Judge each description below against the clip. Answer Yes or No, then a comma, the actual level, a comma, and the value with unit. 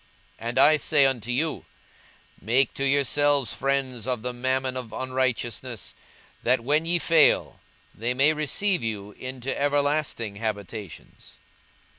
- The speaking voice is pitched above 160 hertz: No, low, 130 Hz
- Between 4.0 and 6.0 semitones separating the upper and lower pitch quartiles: No, average, 3.5 semitones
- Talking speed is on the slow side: Yes, slow, 130 wpm